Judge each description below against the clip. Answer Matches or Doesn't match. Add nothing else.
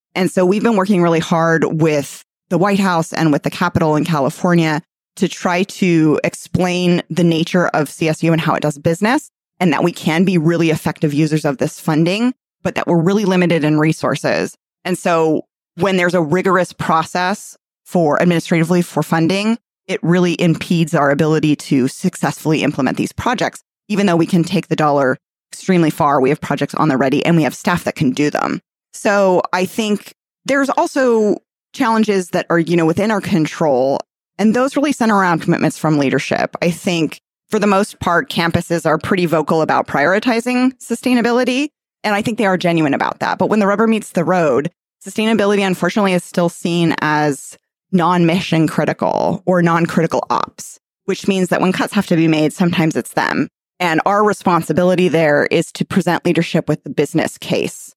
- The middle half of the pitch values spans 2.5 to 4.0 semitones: Matches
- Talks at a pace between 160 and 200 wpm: Matches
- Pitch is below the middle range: Doesn't match